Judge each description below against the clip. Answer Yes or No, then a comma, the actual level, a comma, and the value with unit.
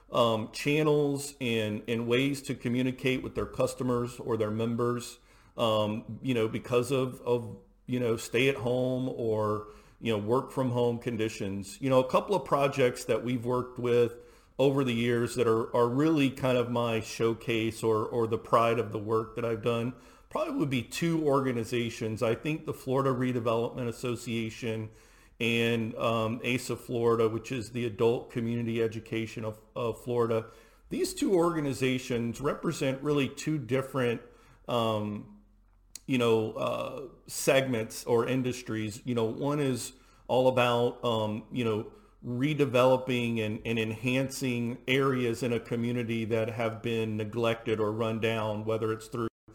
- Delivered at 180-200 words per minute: No, average, 155 wpm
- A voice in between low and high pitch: No, low, 120 Hz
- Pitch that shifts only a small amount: Yes, narrow, 2.3 semitones